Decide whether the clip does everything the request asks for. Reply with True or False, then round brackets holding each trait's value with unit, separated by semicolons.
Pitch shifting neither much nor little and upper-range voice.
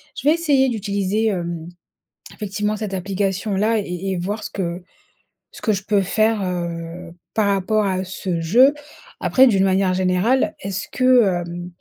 True (3.1 semitones; 195 Hz)